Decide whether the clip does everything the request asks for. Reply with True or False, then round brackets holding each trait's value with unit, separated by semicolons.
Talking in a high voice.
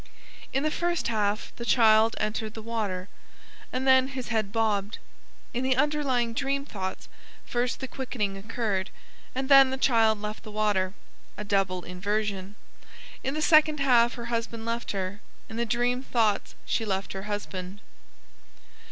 True (225 Hz)